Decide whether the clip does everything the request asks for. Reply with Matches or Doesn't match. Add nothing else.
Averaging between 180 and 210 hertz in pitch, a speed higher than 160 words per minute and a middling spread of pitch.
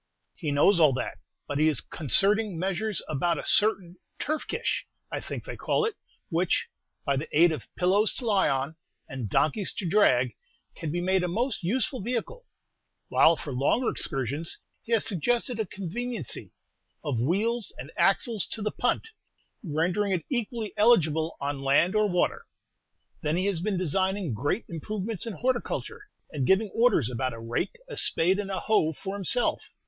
Doesn't match